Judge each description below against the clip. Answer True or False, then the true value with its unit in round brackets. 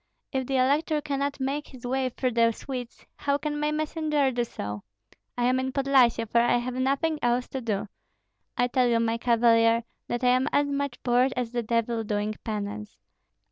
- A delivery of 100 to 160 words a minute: False (190 wpm)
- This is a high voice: True (250 Hz)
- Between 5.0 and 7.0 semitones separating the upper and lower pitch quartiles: False (3.0 semitones)